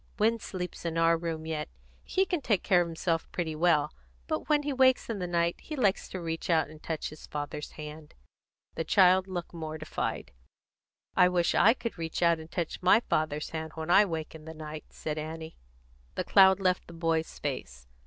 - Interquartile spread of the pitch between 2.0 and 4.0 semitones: Yes, average, 2.9 semitones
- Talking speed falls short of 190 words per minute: No, average, 200 wpm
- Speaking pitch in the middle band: Yes, medium, 165 Hz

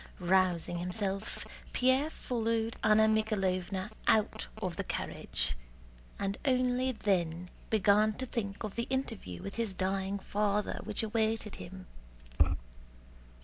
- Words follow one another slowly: Yes, slow, 115 wpm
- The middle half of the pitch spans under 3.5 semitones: Yes, average, 2.9 semitones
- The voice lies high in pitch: Yes, high, 210 Hz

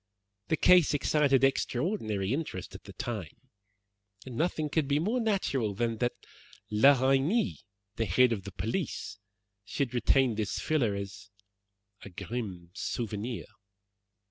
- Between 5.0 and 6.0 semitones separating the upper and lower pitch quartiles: Yes, wide, 5.6 semitones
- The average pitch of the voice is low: Yes, low, 125 Hz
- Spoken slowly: Yes, slow, 130 wpm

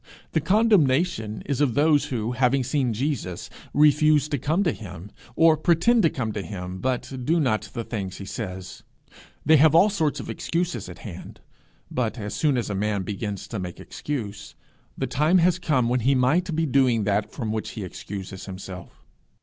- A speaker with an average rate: Yes, average, 185 wpm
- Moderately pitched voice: No, low, 125 Hz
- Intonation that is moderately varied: No, wide, 6.7 semitones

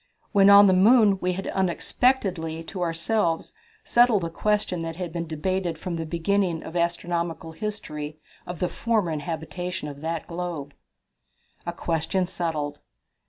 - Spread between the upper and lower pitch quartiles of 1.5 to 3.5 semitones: Yes, average, 2.8 semitones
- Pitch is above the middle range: No, medium, 175 Hz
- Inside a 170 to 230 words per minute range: No, average, 145 wpm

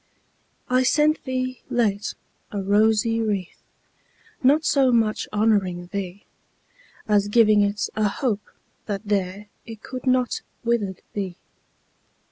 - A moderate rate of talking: No, slow, 115 wpm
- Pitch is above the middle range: Yes, high, 215 Hz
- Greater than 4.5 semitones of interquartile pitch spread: No, average, 3.3 semitones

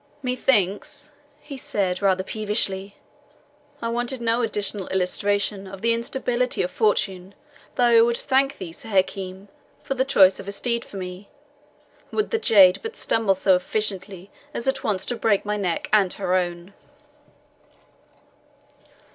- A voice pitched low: No, high, 205 Hz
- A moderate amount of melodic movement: Yes, average, 3.9 semitones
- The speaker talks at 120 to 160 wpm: Yes, average, 145 wpm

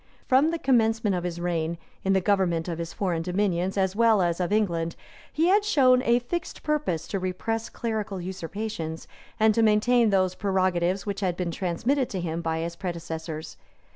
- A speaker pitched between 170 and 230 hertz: Yes, high, 190 Hz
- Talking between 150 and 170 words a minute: No, average, 180 wpm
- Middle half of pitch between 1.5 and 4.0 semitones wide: No, average, 4.5 semitones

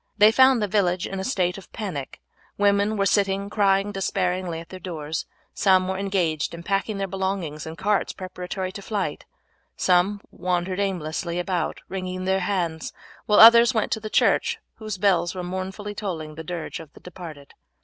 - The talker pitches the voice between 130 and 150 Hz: No, high, 190 Hz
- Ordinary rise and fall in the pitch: No, narrow, 2.3 semitones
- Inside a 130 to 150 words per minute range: No, average, 175 wpm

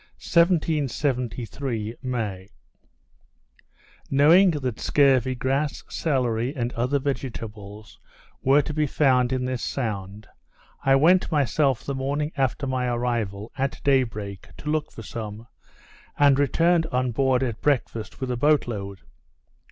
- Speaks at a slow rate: Yes, slow, 130 wpm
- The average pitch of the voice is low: Yes, low, 130 Hz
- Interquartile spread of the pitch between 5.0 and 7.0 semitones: No, average, 3.7 semitones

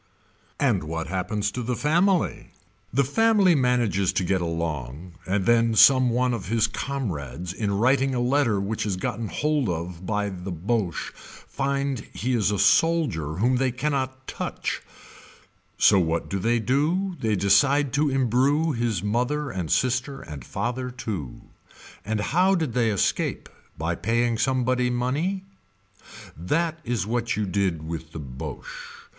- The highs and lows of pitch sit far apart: Yes, wide, 6.1 semitones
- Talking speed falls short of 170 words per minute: Yes, average, 150 wpm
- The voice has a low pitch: Yes, low, 115 Hz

